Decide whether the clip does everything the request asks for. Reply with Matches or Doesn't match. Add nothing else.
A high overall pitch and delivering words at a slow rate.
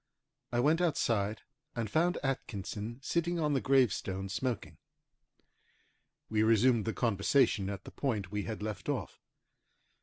Doesn't match